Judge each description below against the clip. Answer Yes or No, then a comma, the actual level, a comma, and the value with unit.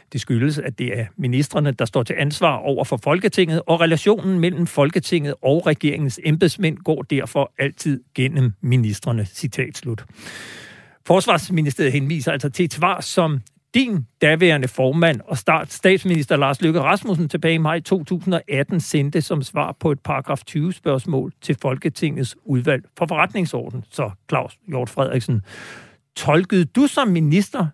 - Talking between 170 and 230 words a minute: No, slow, 145 wpm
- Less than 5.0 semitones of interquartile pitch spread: Yes, average, 4.2 semitones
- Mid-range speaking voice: Yes, medium, 150 Hz